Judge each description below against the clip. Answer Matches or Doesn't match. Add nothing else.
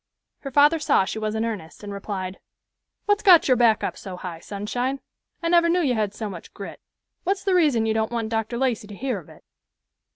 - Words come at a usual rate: Doesn't match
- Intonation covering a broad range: Matches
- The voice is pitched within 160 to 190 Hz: Doesn't match